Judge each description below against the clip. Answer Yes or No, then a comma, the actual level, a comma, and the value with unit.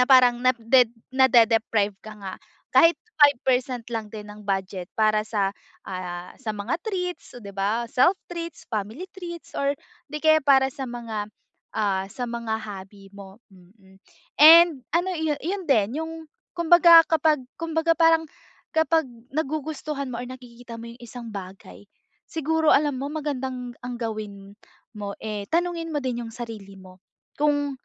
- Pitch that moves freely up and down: Yes, wide, 6.7 semitones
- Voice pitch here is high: Yes, high, 245 Hz